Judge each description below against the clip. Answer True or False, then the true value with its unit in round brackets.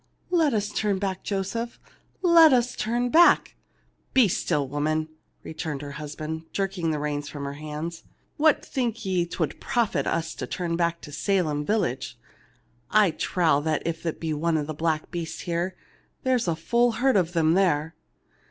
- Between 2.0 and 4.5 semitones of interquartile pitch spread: False (5.5 semitones)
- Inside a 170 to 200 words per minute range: True (175 wpm)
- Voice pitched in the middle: True (170 Hz)